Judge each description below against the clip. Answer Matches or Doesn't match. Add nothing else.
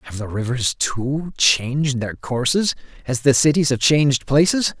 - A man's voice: Matches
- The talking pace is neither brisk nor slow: Matches